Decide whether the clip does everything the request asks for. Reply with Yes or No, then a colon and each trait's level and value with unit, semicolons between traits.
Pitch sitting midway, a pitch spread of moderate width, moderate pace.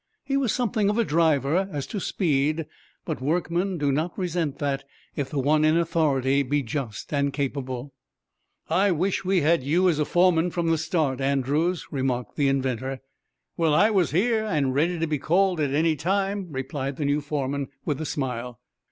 Yes: medium, 155 Hz; average, 4.3 semitones; average, 185 wpm